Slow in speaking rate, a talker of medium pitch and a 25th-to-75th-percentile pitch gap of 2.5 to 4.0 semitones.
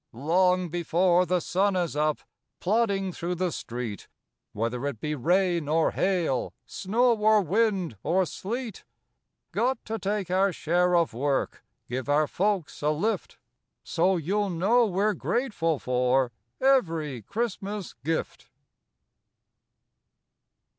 No: slow, 120 wpm; medium, 180 Hz; average, 4.9 semitones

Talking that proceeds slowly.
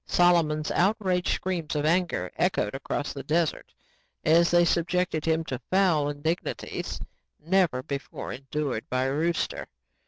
Yes: slow, 130 wpm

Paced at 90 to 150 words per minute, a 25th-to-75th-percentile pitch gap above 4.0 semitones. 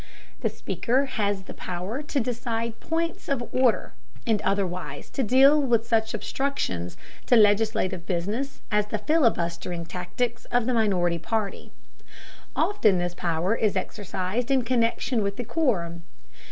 Yes: average, 140 wpm; average, 5.1 semitones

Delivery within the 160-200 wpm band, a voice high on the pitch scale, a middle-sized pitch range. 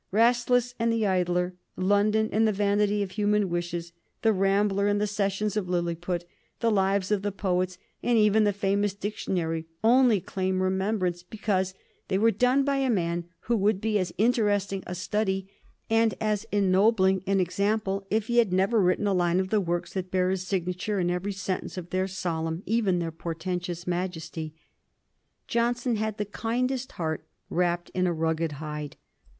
Yes: average, 175 wpm; high, 195 Hz; average, 3.0 semitones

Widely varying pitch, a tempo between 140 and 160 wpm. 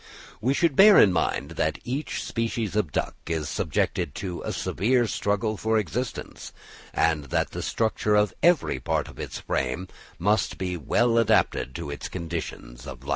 No: wide, 6.1 semitones; average, 170 wpm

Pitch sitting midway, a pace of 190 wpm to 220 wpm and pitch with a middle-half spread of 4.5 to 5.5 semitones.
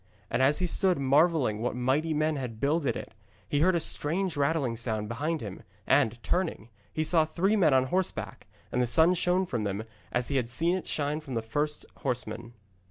Yes: medium, 145 Hz; average, 200 wpm; average, 5.2 semitones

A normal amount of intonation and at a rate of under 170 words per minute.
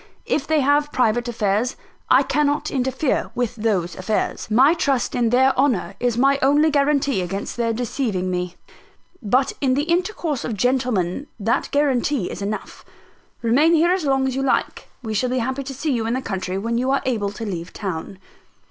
No: average, 4.5 semitones; average, 185 wpm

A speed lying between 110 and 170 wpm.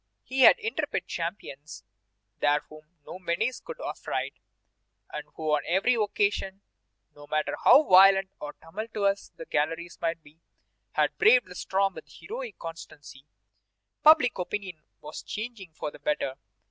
Yes: average, 140 wpm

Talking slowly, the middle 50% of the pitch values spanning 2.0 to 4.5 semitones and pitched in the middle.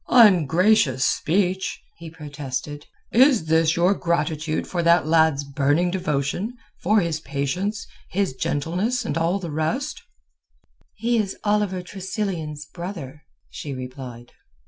No: slow, 120 wpm; average, 5.1 semitones; medium, 170 Hz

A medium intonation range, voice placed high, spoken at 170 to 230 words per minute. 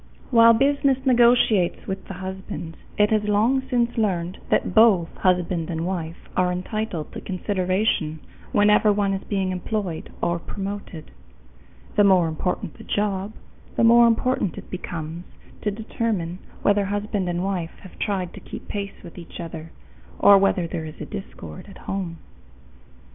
No: average, 3.2 semitones; high, 195 Hz; average, 150 wpm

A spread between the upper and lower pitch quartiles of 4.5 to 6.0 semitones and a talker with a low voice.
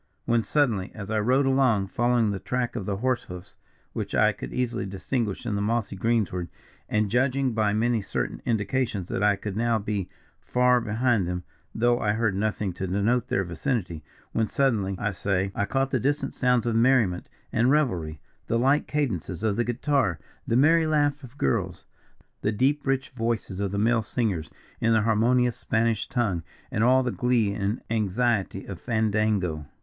No: average, 3.9 semitones; low, 110 Hz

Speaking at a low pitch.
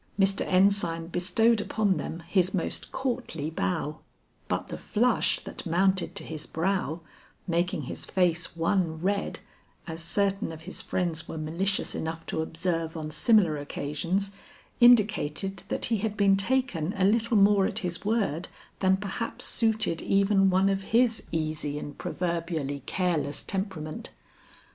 No: medium, 185 Hz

